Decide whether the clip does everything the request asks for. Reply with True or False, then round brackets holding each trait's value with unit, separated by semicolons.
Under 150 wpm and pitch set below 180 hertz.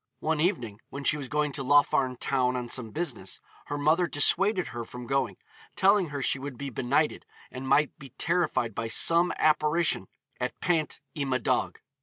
False (175 wpm; 140 Hz)